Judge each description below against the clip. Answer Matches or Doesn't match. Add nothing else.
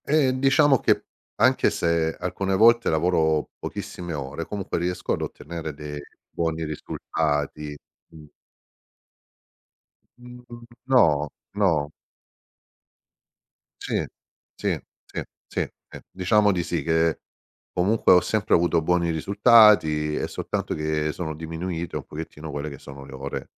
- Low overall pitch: Matches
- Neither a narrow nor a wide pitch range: Matches